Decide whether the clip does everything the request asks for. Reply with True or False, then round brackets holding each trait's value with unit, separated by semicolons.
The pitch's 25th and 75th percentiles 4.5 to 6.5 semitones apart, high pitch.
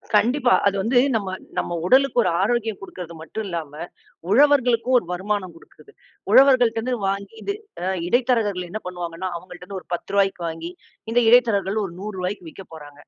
True (5.1 semitones; 200 Hz)